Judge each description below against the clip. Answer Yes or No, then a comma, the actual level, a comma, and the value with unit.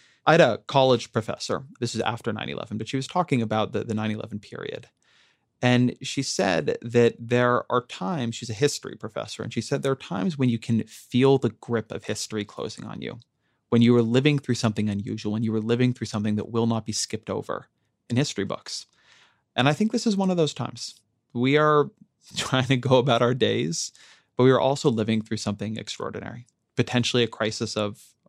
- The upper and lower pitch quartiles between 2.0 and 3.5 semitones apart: Yes, average, 3.1 semitones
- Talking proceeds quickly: Yes, fast, 210 wpm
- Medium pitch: No, low, 120 Hz